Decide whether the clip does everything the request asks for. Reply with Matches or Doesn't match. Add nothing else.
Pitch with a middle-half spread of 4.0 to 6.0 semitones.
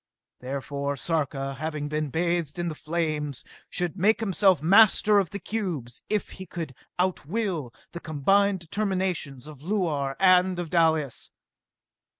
Matches